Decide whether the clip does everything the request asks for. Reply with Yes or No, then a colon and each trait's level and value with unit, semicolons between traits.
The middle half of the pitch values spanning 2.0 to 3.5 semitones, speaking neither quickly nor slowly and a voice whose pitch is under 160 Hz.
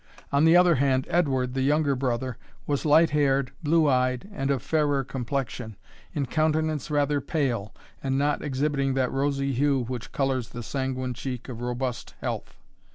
Yes: narrow, 2.4 semitones; average, 160 wpm; low, 135 Hz